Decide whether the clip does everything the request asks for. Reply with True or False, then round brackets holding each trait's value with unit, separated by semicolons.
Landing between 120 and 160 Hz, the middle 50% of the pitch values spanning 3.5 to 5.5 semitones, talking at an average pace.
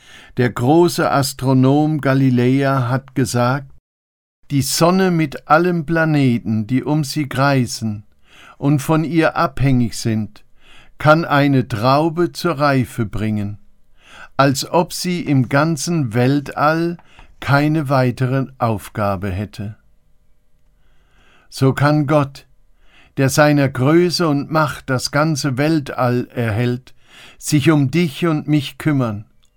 False (135 Hz; 3.9 semitones; 110 wpm)